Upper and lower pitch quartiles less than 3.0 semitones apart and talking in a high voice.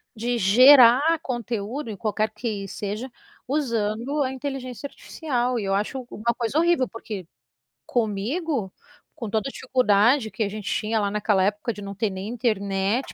No: average, 3.8 semitones; high, 230 Hz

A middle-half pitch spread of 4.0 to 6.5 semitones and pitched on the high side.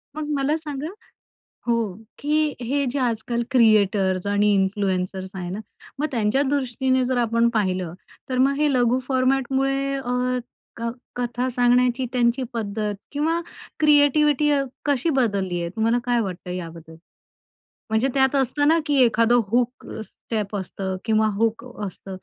Yes: average, 4.6 semitones; high, 240 Hz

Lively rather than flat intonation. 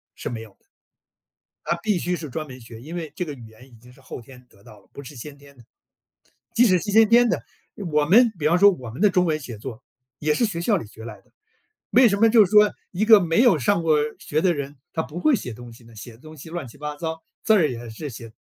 Yes: wide, 7.0 semitones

